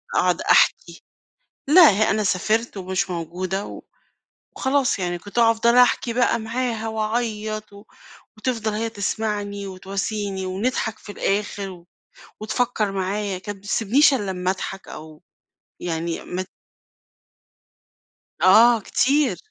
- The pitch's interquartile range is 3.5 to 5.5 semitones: No, average, 3.1 semitones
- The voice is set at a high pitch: Yes, high, 210 Hz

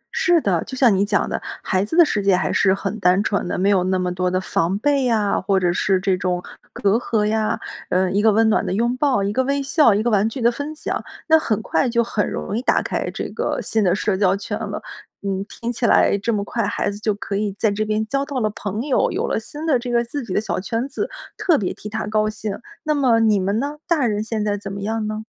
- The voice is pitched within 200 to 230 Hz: Yes, high, 215 Hz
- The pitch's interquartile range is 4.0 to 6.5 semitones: No, average, 3.3 semitones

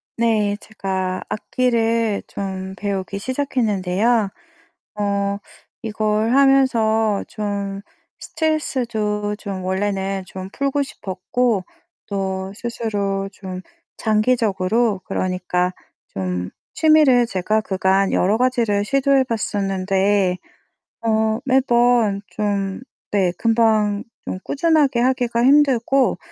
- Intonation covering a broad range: No, average, 3.6 semitones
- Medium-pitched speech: No, high, 210 Hz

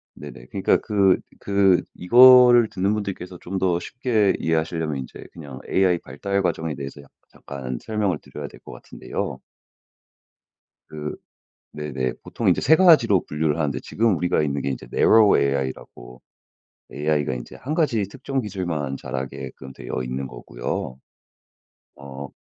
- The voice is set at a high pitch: No, very low, 80 Hz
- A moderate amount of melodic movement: No, wide, 6.6 semitones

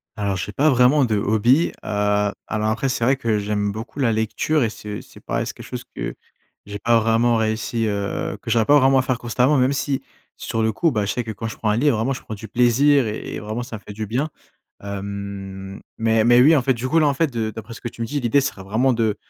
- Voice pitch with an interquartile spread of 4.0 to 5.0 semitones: No, average, 3.6 semitones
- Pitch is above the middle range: No, low, 115 Hz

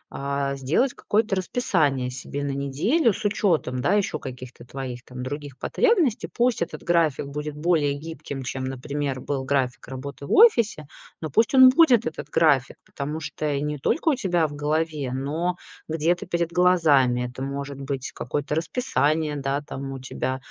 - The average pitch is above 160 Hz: No, medium, 145 Hz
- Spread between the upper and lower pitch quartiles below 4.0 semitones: No, average, 4.3 semitones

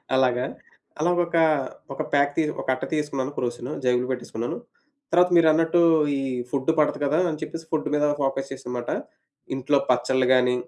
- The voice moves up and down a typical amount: Yes, average, 3.3 semitones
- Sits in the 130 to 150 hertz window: Yes, low, 135 Hz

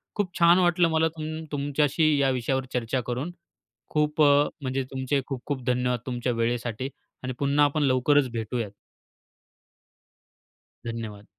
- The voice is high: No, low, 135 Hz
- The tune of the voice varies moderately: Yes, average, 3.4 semitones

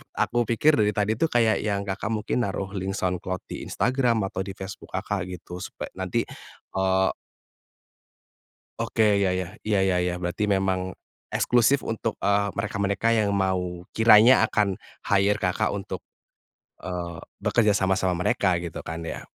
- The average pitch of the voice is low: Yes, low, 100 Hz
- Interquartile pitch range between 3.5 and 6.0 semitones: No, average, 2.8 semitones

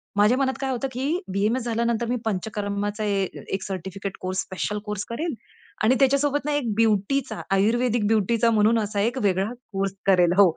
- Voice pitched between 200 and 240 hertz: Yes, high, 215 Hz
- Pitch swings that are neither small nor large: Yes, average, 3.6 semitones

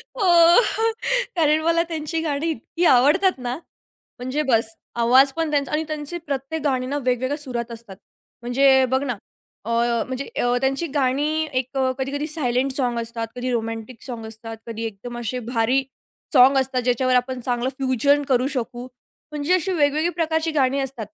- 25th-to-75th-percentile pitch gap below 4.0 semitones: Yes, average, 3.4 semitones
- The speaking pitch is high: Yes, very high, 265 Hz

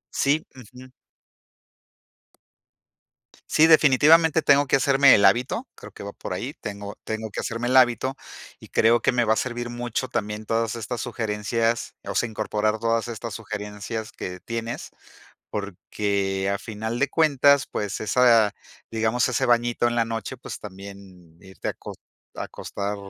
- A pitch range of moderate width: Yes, average, 3.2 semitones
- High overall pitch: No, low, 115 Hz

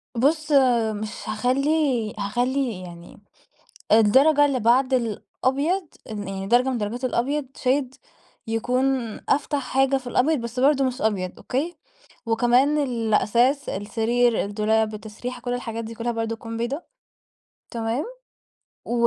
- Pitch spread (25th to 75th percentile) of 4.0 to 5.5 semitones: No, average, 3.4 semitones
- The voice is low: No, high, 245 Hz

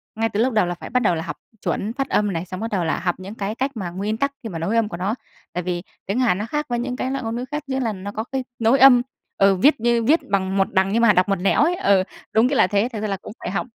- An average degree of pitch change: Yes, average, 4.4 semitones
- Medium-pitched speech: No, high, 215 Hz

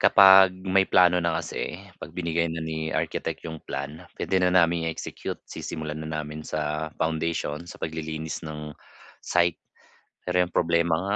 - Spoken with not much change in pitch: Yes, narrow, 2.2 semitones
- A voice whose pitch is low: Yes, very low, 80 Hz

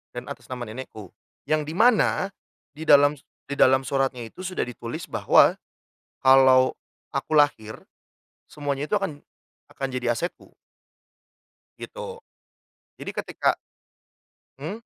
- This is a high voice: No, medium, 140 Hz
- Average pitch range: Yes, average, 3.8 semitones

